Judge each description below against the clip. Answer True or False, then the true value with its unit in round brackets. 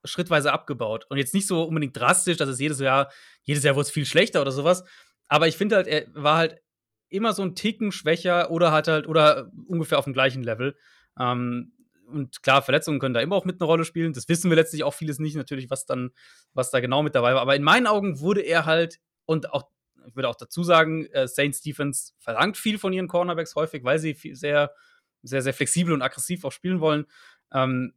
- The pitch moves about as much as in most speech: True (3.9 semitones)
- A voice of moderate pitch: True (155 Hz)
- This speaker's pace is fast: True (220 wpm)